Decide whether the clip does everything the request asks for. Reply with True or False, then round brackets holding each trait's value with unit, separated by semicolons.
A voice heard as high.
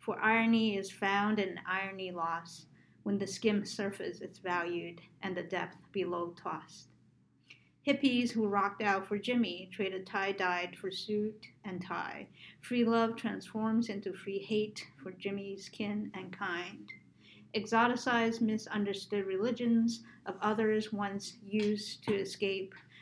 True (200 Hz)